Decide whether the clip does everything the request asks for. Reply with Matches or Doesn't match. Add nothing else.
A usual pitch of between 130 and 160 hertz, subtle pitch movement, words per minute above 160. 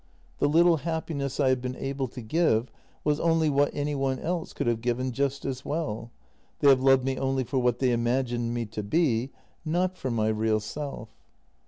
Doesn't match